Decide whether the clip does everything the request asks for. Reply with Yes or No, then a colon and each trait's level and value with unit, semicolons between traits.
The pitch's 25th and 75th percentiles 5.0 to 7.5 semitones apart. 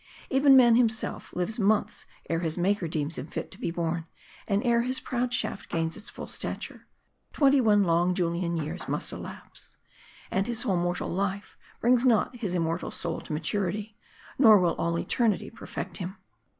Yes: wide, 5.4 semitones